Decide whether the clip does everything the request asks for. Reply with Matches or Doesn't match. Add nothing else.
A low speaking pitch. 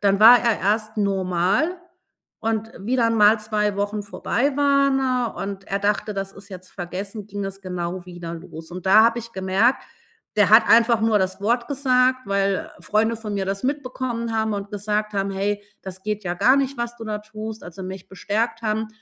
Doesn't match